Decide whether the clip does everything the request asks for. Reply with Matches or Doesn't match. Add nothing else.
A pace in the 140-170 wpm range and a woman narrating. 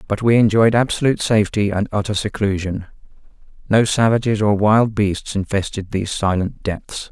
Doesn't match